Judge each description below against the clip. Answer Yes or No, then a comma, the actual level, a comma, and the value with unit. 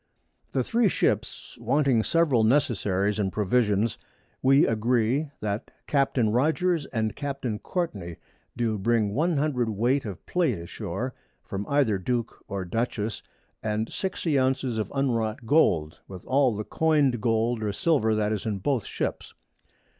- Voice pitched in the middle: No, low, 115 Hz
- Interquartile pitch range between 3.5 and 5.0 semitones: Yes, average, 4.7 semitones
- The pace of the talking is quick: No, average, 145 wpm